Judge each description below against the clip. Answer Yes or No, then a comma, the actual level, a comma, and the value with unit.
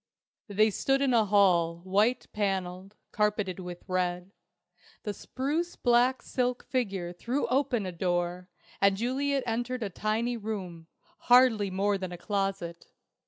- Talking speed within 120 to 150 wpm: Yes, slow, 135 wpm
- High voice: Yes, high, 205 Hz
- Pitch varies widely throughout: No, average, 4.8 semitones